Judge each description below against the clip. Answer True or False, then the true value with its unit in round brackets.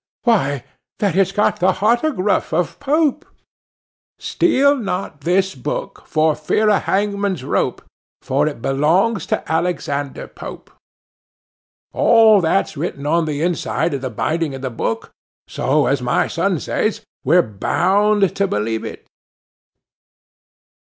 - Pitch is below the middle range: False (175 Hz)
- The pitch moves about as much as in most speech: False (6.2 semitones)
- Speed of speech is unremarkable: False (130 wpm)